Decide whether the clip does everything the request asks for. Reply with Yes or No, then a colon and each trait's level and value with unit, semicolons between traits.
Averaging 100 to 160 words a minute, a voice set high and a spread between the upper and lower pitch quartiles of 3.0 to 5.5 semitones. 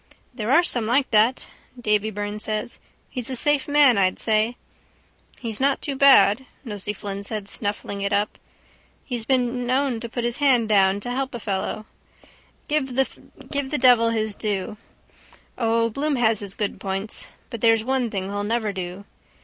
No: average, 170 wpm; high, 225 Hz; average, 3.5 semitones